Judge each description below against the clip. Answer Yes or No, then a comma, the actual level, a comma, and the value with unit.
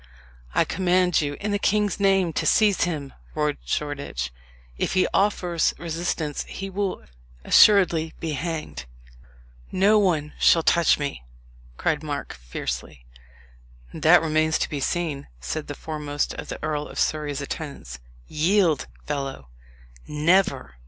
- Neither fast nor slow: No, slow, 130 wpm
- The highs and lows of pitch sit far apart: No, average, 3.9 semitones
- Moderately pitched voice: Yes, medium, 155 Hz